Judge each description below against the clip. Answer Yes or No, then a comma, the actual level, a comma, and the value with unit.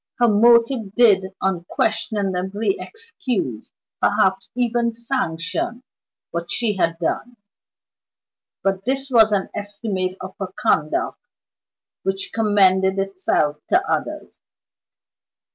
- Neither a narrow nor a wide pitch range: Yes, average, 3.8 semitones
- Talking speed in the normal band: No, slow, 95 wpm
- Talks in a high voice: Yes, high, 205 Hz